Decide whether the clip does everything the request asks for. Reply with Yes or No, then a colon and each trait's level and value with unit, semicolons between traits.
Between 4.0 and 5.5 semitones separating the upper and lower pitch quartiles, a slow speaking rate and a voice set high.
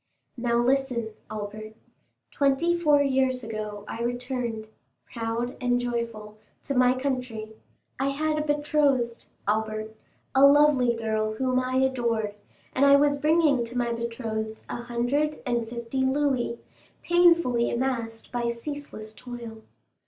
No: average, 3.3 semitones; slow, 130 wpm; high, 245 Hz